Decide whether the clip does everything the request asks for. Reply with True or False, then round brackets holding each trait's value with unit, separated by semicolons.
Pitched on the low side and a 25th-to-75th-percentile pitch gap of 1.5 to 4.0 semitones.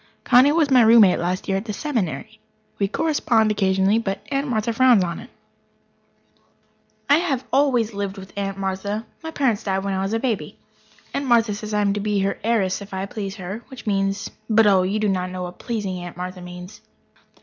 False (205 Hz; 3.3 semitones)